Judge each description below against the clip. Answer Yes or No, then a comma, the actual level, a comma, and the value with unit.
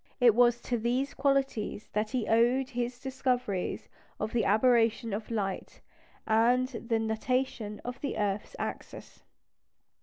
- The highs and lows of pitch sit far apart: No, narrow, 2.6 semitones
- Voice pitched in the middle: No, high, 235 Hz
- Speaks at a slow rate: Yes, slow, 130 wpm